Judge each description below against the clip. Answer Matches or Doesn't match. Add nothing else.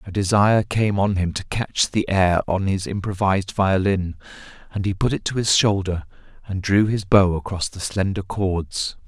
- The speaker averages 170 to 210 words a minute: Matches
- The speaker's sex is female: Doesn't match